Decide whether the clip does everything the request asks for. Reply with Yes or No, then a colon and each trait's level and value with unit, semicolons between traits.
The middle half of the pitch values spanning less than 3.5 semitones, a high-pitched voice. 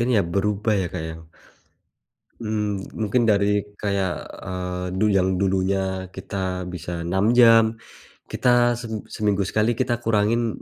No: average, 2.9 semitones; low, 100 Hz